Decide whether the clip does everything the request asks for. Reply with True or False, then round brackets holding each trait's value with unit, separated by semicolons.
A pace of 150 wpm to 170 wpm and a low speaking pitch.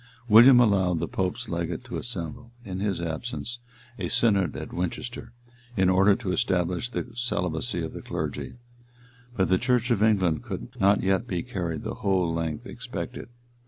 True (160 wpm; 95 Hz)